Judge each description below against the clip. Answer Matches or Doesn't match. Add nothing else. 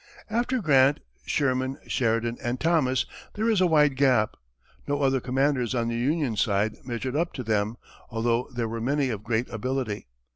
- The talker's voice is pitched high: Doesn't match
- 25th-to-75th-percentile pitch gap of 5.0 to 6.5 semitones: Doesn't match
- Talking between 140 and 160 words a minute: Doesn't match